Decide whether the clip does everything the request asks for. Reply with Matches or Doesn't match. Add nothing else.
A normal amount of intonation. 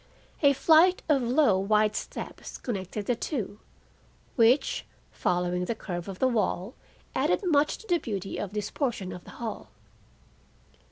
Doesn't match